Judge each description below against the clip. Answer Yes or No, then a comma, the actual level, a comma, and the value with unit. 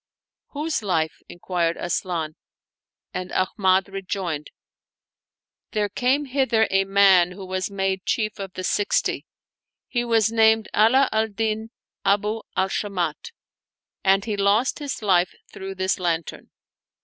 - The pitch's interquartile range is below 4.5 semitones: Yes, average, 3.0 semitones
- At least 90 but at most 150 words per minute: Yes, slow, 135 wpm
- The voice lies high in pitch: Yes, high, 200 Hz